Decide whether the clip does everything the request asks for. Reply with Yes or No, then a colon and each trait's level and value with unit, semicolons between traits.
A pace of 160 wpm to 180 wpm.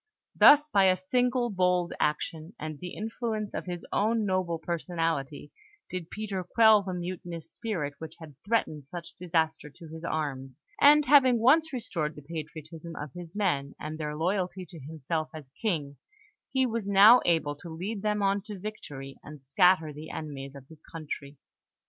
Yes: average, 165 wpm